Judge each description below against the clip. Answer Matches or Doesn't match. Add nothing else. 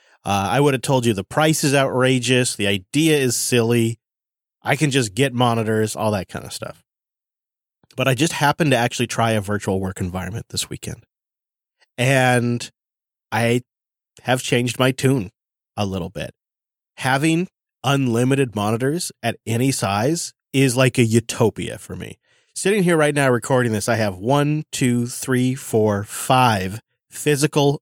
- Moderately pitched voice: Doesn't match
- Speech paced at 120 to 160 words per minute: Matches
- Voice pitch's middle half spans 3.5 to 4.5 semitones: Matches